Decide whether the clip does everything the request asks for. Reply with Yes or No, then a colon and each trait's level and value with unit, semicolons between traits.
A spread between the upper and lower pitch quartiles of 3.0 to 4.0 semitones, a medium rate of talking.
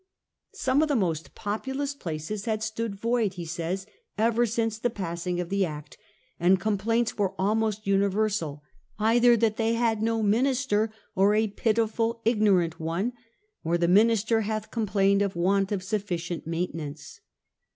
Yes: average, 3.7 semitones; average, 150 wpm